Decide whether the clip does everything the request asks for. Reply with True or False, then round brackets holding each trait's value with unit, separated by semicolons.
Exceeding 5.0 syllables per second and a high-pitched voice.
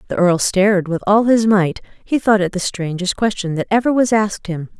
True (5.3 syllables/s; 200 Hz)